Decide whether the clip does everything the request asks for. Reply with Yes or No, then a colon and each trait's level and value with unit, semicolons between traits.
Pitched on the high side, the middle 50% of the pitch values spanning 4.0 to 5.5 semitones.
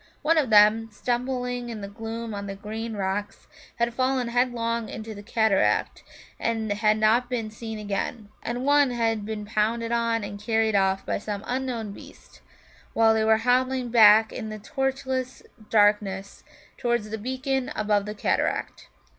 No: high, 225 Hz; narrow, 2.6 semitones